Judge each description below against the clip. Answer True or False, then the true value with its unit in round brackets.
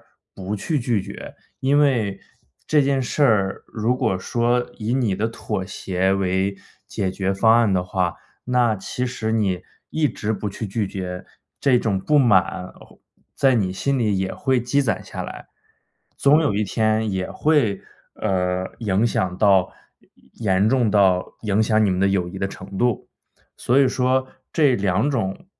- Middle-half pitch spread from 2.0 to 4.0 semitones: False (4.6 semitones)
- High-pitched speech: False (110 Hz)